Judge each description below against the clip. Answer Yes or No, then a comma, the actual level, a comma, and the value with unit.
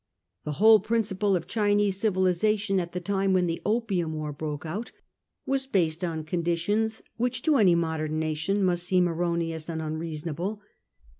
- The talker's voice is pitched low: No, medium, 180 Hz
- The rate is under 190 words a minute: Yes, average, 155 wpm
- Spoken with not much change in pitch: No, average, 4.2 semitones